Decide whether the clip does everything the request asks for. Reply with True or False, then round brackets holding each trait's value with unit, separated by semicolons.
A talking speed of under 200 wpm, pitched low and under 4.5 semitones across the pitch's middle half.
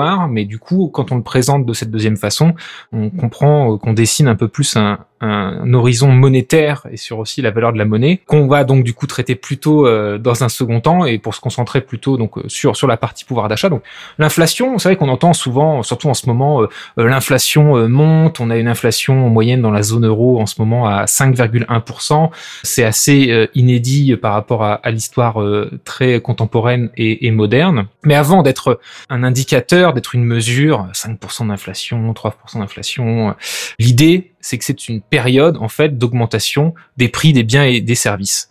True (185 wpm; 125 Hz; 4.1 semitones)